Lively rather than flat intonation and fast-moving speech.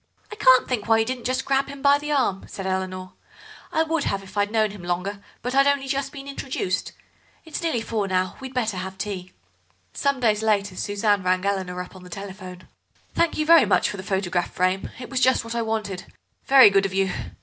Yes: wide, 5.7 semitones; fast, 215 wpm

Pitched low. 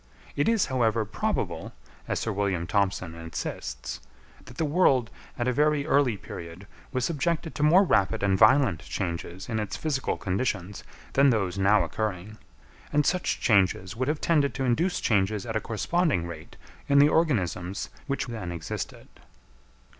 Yes: low, 110 Hz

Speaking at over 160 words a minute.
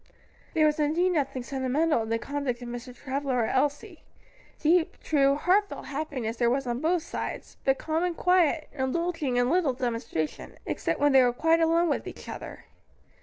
Yes: average, 175 wpm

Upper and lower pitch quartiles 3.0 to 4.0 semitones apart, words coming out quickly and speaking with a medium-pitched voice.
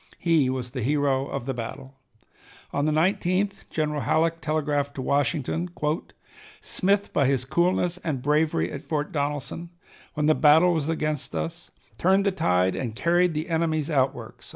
No: average, 3.5 semitones; average, 155 wpm; medium, 150 Hz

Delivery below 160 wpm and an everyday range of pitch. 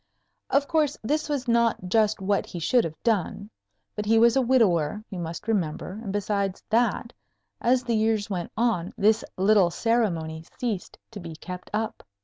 No: average, 170 wpm; average, 4.3 semitones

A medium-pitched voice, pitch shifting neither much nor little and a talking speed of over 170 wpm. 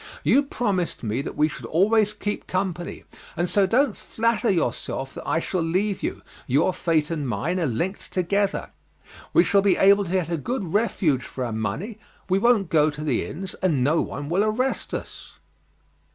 Yes: medium, 180 Hz; average, 5.0 semitones; average, 185 wpm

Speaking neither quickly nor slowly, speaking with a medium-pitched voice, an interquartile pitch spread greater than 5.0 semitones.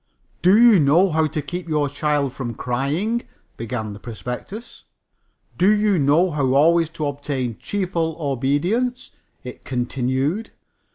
No: slow, 130 wpm; medium, 150 Hz; wide, 5.5 semitones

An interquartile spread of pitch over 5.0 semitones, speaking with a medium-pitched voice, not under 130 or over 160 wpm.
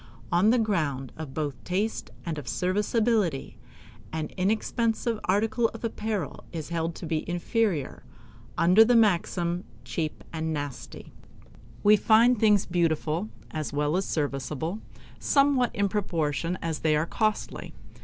Yes: wide, 5.5 semitones; medium, 180 Hz; slow, 135 wpm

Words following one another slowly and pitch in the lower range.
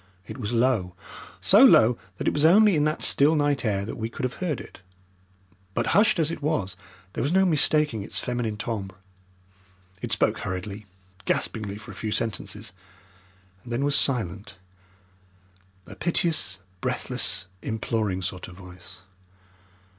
No: average, 155 wpm; low, 115 Hz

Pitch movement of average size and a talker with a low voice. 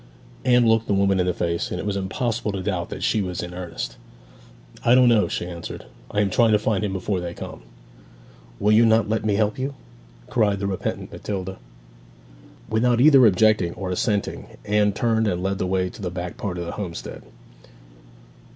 Yes: average, 3.3 semitones; low, 100 Hz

